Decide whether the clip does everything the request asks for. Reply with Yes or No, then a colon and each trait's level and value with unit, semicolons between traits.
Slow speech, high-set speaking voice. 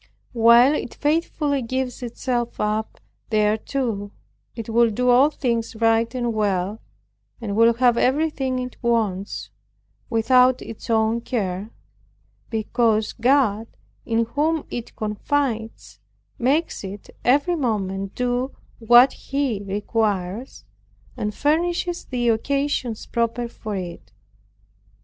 Yes: slow, 110 wpm; high, 235 Hz